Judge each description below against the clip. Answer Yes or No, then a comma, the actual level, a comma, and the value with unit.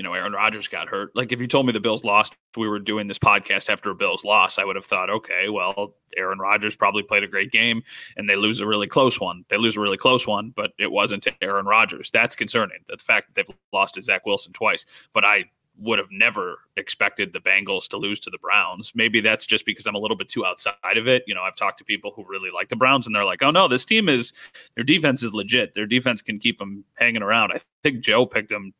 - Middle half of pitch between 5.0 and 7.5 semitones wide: No, average, 3.8 semitones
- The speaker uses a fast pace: Yes, fast, 265 wpm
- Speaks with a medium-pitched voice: No, low, 110 Hz